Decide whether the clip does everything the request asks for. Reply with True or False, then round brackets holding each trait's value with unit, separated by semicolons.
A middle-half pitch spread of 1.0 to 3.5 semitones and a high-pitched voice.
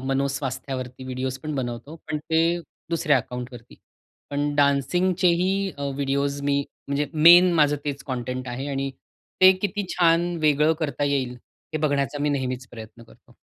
False (2.9 semitones; 140 Hz)